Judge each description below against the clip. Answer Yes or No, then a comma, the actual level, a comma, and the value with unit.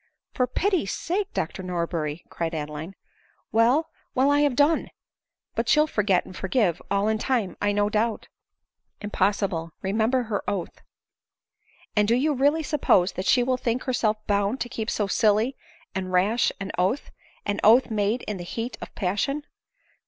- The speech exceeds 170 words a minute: Yes, average, 180 wpm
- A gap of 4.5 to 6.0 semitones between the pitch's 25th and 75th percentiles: Yes, average, 4.8 semitones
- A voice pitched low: No, high, 215 Hz